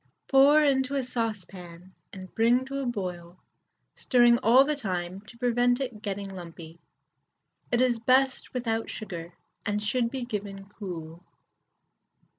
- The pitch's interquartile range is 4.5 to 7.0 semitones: Yes, average, 5.3 semitones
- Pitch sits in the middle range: No, high, 225 Hz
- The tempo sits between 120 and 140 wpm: Yes, slow, 135 wpm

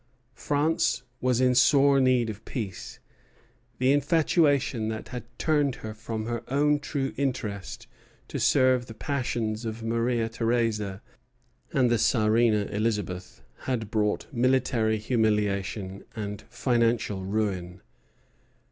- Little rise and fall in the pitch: No, average, 3.1 semitones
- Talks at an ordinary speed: No, slow, 115 wpm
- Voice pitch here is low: Yes, low, 115 Hz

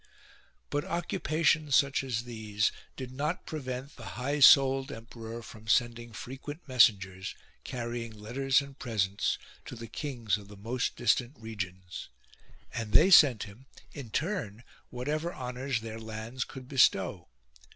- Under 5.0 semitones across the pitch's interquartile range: Yes, average, 3.7 semitones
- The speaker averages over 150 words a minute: No, average, 140 wpm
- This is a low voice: Yes, low, 120 Hz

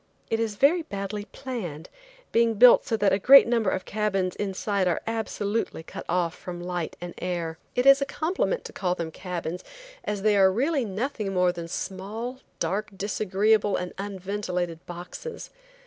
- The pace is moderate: Yes, average, 165 wpm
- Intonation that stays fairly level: No, average, 3.9 semitones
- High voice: Yes, high, 200 Hz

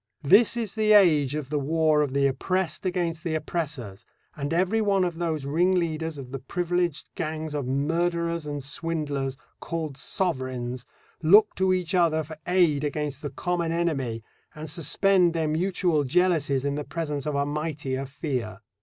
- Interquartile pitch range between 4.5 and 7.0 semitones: No, average, 3.7 semitones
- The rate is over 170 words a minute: No, average, 165 wpm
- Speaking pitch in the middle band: Yes, medium, 155 Hz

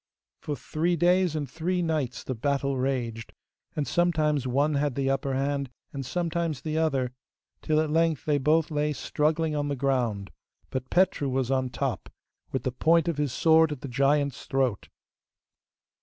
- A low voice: No, medium, 145 Hz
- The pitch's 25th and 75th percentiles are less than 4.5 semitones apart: Yes, average, 3.2 semitones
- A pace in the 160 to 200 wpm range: Yes, average, 170 wpm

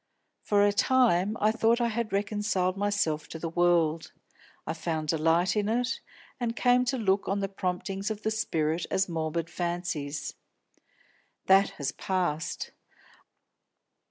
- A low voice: No, high, 190 Hz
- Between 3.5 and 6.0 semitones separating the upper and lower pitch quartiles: Yes, average, 4.4 semitones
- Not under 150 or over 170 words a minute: No, average, 140 wpm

